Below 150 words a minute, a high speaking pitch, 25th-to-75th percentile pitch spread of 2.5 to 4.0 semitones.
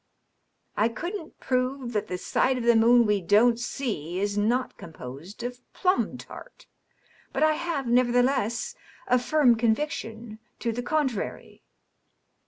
Yes: average, 140 wpm; high, 240 Hz; average, 3.4 semitones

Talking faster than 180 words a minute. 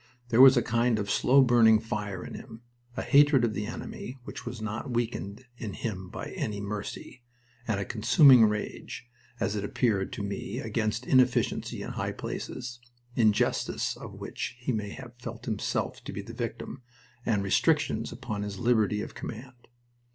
No: average, 170 wpm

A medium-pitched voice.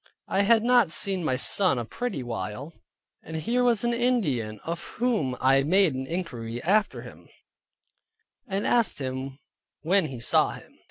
Yes: medium, 165 Hz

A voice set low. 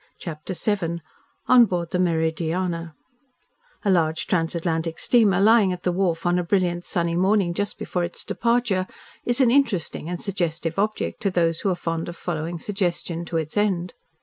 No: medium, 175 Hz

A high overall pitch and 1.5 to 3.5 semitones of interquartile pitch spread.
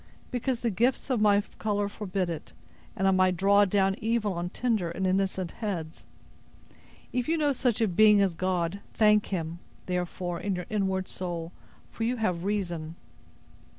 Yes: high, 195 Hz; average, 3.2 semitones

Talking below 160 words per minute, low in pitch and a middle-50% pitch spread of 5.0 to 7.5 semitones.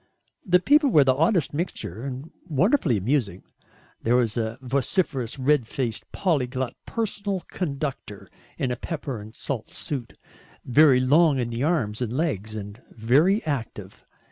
Yes: average, 140 wpm; low, 130 Hz; wide, 5.5 semitones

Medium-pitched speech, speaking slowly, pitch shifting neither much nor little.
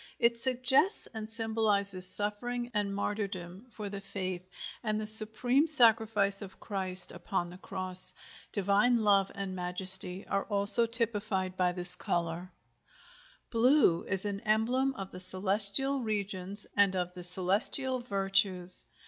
No: high, 200 Hz; slow, 130 wpm; average, 3.3 semitones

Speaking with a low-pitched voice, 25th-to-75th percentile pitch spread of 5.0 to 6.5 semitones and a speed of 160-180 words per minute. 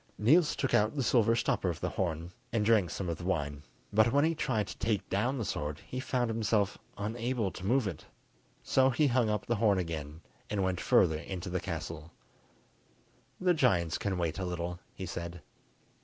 No: low, 100 Hz; wide, 5.4 semitones; average, 200 wpm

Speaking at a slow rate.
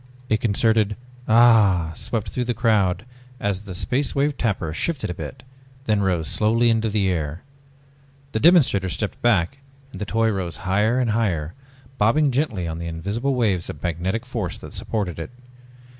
No: average, 165 wpm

